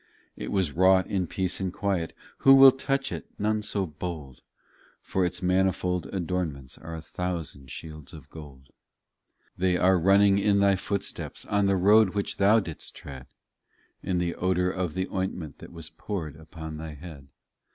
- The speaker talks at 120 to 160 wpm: No, average, 170 wpm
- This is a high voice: No, very low, 90 Hz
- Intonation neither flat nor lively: Yes, average, 3.6 semitones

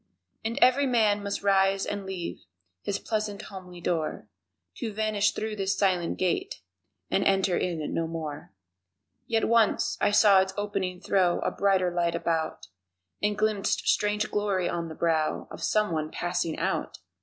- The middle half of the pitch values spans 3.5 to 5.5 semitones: No, average, 3.1 semitones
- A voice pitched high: Yes, high, 195 Hz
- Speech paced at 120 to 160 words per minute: Yes, average, 155 wpm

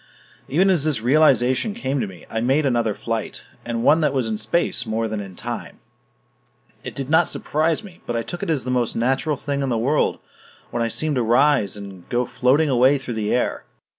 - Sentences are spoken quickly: Yes, fast, 215 wpm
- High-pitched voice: No, low, 125 Hz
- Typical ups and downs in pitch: Yes, average, 4.5 semitones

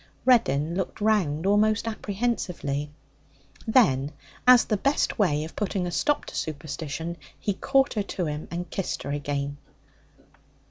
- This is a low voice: No, medium, 180 Hz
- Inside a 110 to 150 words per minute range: Yes, average, 140 wpm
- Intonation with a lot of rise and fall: Yes, wide, 6.6 semitones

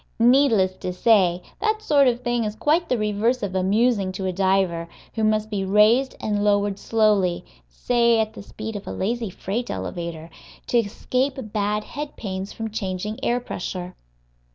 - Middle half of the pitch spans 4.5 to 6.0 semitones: No, average, 3.9 semitones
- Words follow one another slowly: No, average, 170 wpm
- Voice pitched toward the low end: No, high, 210 Hz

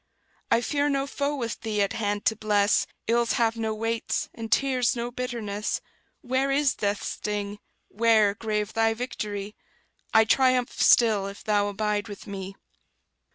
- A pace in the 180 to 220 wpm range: No, average, 155 wpm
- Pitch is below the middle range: No, high, 220 Hz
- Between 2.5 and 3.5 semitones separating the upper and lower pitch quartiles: Yes, average, 2.8 semitones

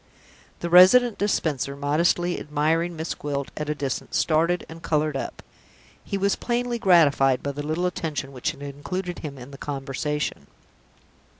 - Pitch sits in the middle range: Yes, medium, 155 Hz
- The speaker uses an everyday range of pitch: Yes, average, 3.8 semitones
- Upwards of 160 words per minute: No, average, 155 wpm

